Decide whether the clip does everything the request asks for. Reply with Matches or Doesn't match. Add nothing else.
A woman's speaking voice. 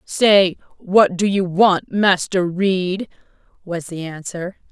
Matches